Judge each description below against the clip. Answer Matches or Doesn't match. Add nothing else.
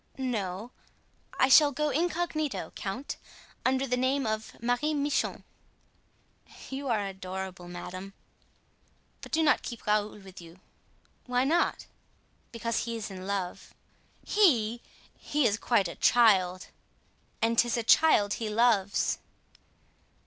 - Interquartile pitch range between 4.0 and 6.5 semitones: Matches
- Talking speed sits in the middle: Doesn't match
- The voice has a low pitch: Doesn't match